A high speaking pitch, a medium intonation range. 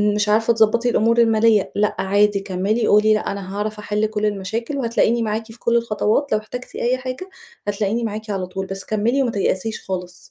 No: high, 215 Hz; narrow, 2.2 semitones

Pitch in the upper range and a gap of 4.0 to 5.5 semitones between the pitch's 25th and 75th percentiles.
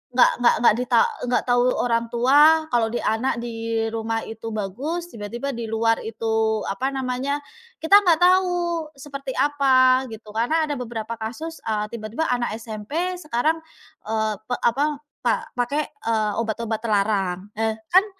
Yes: high, 240 Hz; average, 4.4 semitones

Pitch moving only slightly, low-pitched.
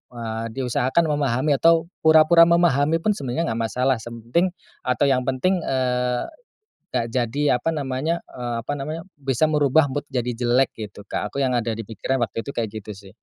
No: average, 4.0 semitones; low, 130 Hz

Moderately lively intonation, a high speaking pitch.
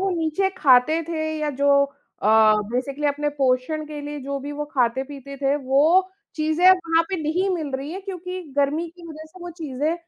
Yes: average, 3.0 semitones; very high, 300 Hz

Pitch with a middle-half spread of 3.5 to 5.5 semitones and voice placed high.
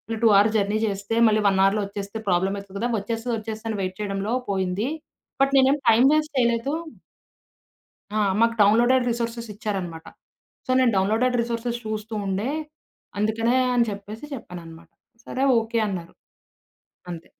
No: average, 3.0 semitones; high, 215 Hz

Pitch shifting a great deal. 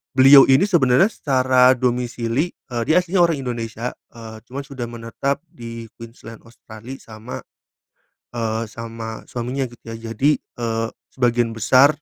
No: narrow, 2.6 semitones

